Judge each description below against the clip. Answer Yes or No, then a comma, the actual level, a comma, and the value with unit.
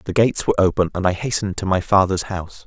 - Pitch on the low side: Yes, very low, 95 Hz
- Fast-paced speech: Yes, fast, 245 wpm